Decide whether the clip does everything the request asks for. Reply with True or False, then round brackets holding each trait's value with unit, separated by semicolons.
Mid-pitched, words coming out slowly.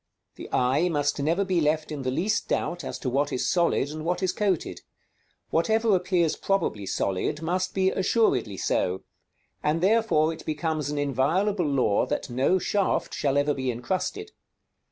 False (160 Hz; 165 wpm)